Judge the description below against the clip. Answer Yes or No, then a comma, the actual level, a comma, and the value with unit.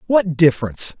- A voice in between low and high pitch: Yes, medium, 165 Hz